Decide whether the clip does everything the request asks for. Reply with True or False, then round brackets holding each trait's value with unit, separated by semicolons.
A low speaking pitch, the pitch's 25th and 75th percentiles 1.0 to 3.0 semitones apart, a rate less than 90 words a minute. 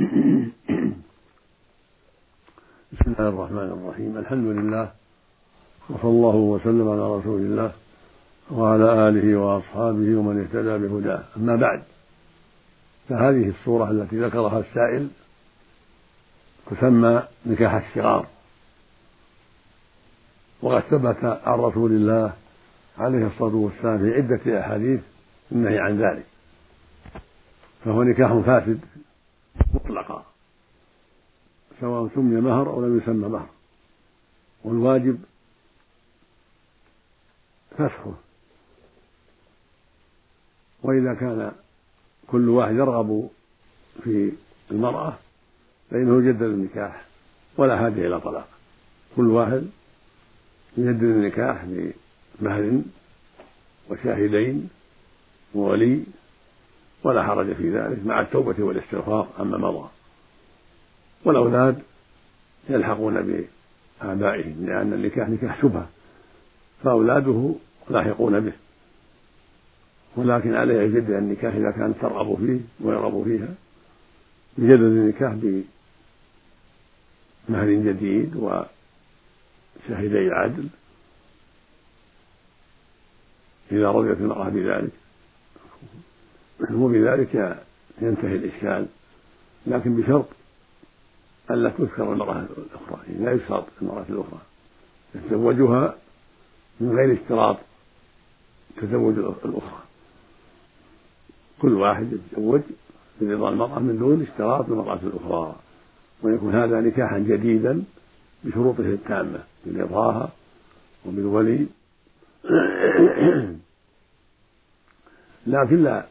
True (110 Hz; 2.4 semitones; 80 wpm)